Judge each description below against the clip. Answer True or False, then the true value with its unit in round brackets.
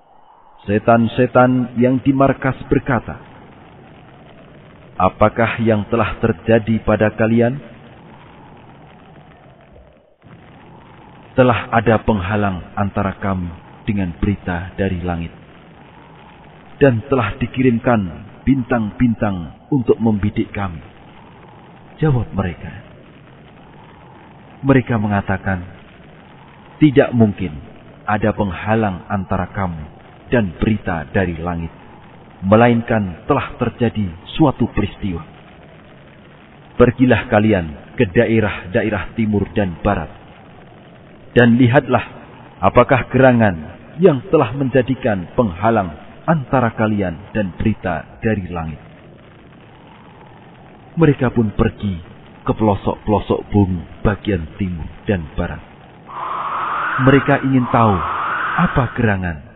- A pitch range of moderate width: True (4.2 semitones)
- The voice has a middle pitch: False (110 Hz)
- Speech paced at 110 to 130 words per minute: False (85 wpm)